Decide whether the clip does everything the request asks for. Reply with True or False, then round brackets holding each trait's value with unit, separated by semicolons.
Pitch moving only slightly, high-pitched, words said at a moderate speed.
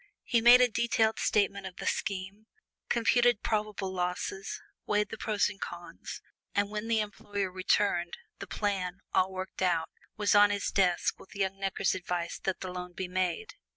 True (2.2 semitones; 195 Hz; 170 wpm)